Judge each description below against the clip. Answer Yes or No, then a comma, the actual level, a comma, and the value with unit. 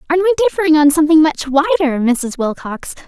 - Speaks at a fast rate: No, average, 175 wpm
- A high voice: Yes, very high, 310 Hz